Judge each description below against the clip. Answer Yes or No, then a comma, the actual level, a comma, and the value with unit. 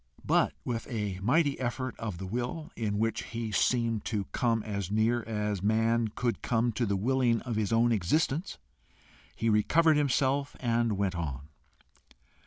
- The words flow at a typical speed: Yes, average, 160 wpm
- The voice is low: Yes, low, 115 Hz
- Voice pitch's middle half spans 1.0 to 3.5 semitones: Yes, average, 2.9 semitones